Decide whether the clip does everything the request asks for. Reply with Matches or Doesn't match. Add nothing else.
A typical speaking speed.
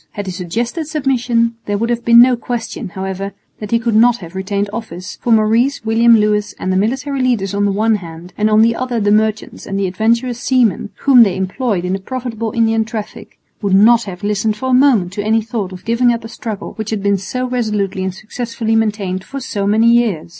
Doesn't match